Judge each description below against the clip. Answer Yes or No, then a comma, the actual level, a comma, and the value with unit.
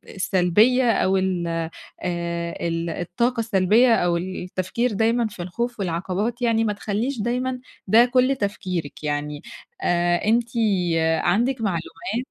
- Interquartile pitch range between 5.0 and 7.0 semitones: Yes, average, 5.3 semitones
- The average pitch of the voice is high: Yes, high, 195 Hz